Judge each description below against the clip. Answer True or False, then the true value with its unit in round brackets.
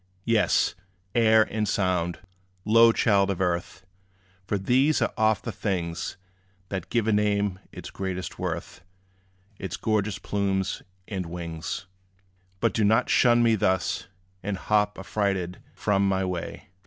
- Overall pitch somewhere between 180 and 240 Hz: False (100 Hz)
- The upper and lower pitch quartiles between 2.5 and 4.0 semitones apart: True (2.8 semitones)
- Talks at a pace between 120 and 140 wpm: True (135 wpm)